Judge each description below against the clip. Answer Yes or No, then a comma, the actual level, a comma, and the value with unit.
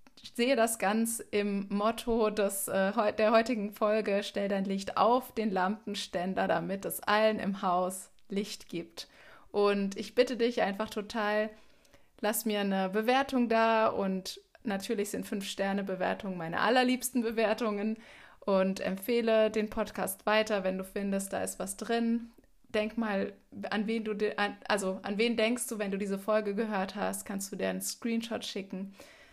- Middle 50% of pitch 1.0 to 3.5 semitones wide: Yes, narrow, 2.4 semitones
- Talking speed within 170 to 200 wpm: No, average, 155 wpm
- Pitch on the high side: Yes, high, 210 Hz